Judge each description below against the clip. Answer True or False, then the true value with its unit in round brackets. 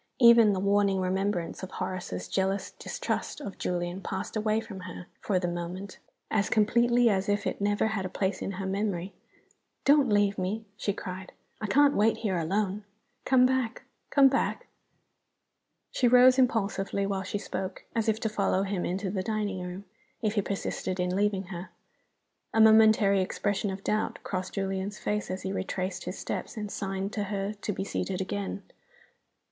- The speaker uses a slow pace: False (175 wpm)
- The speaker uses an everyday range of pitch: False (2.2 semitones)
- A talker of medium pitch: False (200 Hz)